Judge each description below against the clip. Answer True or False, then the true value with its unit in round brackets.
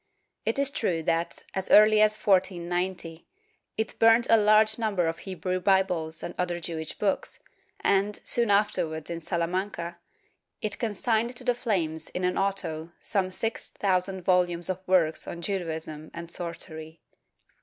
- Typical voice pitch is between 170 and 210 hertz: True (185 Hz)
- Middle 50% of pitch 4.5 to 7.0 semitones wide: False (3.7 semitones)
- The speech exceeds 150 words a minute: False (145 wpm)